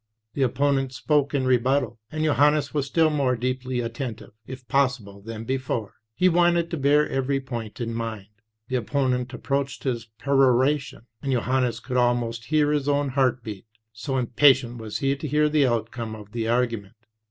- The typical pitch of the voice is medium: No, low, 130 Hz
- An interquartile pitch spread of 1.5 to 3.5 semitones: Yes, average, 3.2 semitones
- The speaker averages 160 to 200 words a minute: Yes, average, 175 wpm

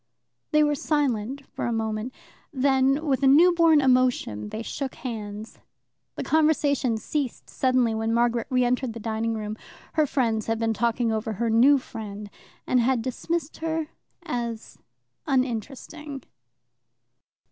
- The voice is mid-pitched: No, very high, 250 Hz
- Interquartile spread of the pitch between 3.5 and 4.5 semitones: Yes, average, 4.0 semitones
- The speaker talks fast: No, slow, 135 wpm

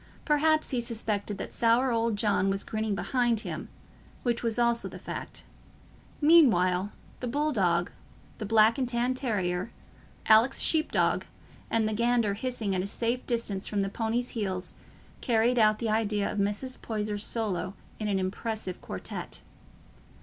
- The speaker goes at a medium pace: Yes, average, 150 wpm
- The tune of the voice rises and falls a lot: No, average, 3.1 semitones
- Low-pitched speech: No, high, 220 Hz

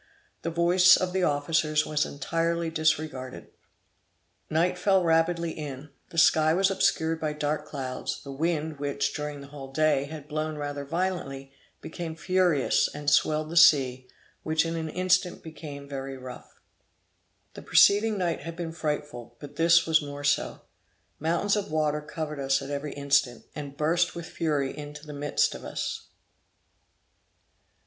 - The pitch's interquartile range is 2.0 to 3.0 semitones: Yes, average, 2.7 semitones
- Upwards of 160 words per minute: No, average, 155 wpm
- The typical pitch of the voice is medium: Yes, medium, 155 Hz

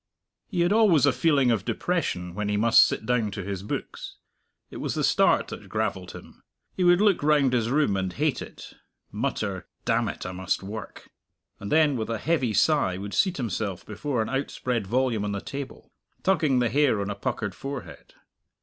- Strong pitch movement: Yes, wide, 6.4 semitones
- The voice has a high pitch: No, low, 120 Hz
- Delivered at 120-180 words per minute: No, average, 195 wpm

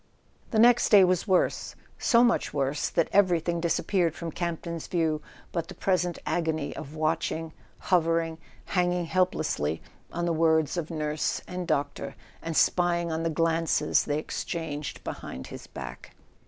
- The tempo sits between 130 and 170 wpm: Yes, average, 155 wpm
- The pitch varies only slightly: Yes, narrow, 2.1 semitones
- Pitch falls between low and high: Yes, medium, 165 Hz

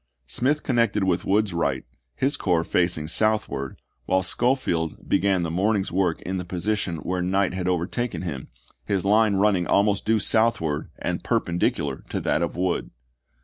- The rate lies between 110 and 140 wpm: No, average, 155 wpm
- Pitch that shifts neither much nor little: Yes, average, 3.6 semitones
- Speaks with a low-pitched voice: Yes, very low, 95 Hz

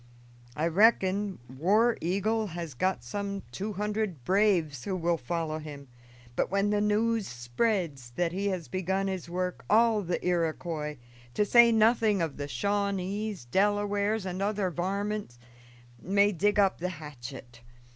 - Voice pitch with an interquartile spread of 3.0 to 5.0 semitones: Yes, average, 3.9 semitones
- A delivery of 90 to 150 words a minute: Yes, average, 145 wpm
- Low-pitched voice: No, high, 190 Hz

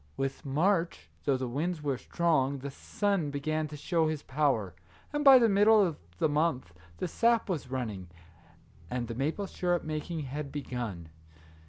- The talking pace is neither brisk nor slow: Yes, average, 165 wpm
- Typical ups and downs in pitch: Yes, average, 4.8 semitones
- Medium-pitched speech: Yes, medium, 150 Hz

